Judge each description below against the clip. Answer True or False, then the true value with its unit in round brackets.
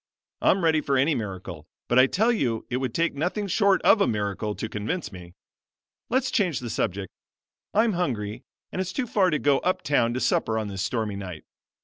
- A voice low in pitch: True (130 Hz)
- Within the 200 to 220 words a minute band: True (205 wpm)